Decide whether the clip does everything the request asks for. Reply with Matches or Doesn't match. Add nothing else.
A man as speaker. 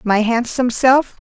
Doesn't match